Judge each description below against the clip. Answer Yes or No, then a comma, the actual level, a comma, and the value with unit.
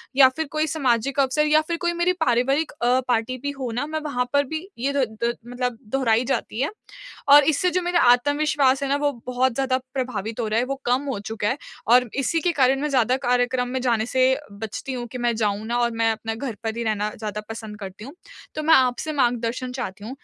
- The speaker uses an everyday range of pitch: Yes, average, 3.6 semitones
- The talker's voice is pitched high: Yes, very high, 255 Hz